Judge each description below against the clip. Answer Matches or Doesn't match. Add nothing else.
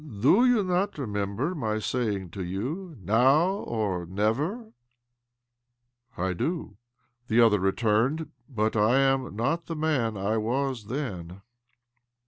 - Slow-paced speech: Doesn't match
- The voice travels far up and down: Matches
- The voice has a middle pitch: Doesn't match